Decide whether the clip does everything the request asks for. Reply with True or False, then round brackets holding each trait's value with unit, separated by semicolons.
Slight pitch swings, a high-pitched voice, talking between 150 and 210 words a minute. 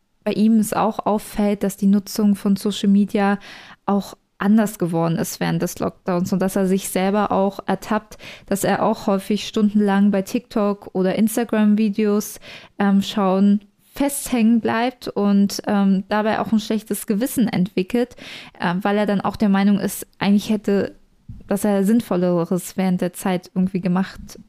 True (1.7 semitones; 205 Hz; 155 wpm)